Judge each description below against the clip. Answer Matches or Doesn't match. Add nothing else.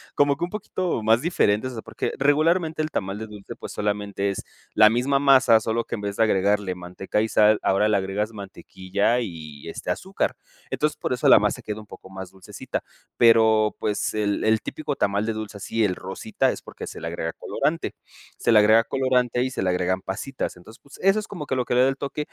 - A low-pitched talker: Matches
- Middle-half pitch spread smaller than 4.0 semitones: Doesn't match